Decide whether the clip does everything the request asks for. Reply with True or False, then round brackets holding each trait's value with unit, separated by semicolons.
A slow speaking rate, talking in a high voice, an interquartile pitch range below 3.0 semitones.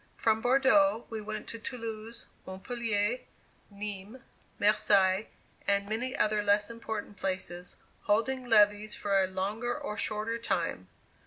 True (120 wpm; 215 Hz; 2.5 semitones)